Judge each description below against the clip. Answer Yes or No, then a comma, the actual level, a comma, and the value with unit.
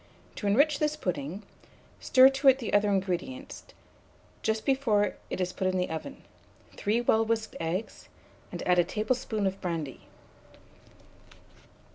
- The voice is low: No, high, 210 Hz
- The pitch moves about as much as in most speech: No, wide, 5.9 semitones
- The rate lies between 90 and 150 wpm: Yes, slow, 135 wpm